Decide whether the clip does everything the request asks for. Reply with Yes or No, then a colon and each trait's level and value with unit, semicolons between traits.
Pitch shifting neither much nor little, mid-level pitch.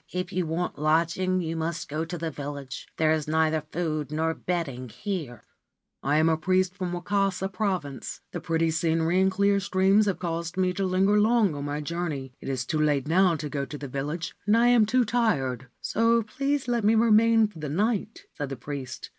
Yes: average, 4.5 semitones; medium, 170 Hz